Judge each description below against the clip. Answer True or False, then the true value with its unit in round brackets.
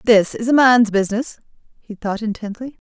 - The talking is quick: False (170 wpm)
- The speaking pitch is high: True (225 Hz)